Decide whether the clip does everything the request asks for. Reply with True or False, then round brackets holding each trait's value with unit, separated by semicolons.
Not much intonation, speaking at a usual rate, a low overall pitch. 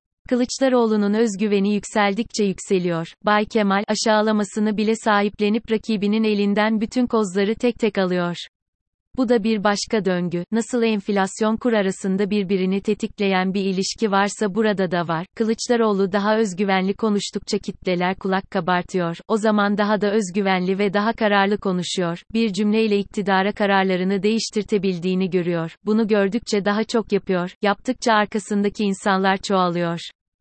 False (2.2 semitones; 125 wpm; 205 Hz)